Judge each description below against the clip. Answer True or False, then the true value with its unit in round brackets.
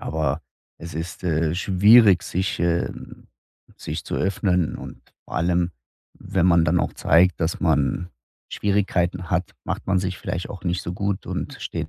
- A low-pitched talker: True (90 Hz)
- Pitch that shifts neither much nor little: False (1.9 semitones)